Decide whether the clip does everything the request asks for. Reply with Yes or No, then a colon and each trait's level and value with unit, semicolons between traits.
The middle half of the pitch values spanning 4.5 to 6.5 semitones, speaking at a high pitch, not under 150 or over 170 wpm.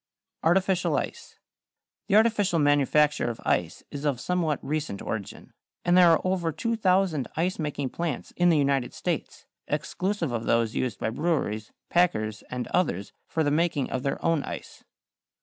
No: average, 5.2 semitones; medium, 155 Hz; average, 155 wpm